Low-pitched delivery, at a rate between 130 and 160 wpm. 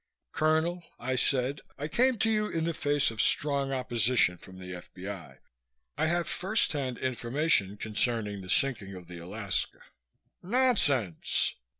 Yes: low, 130 Hz; average, 140 wpm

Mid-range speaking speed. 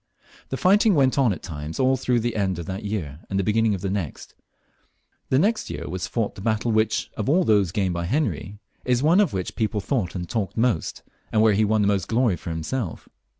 No: fast, 235 wpm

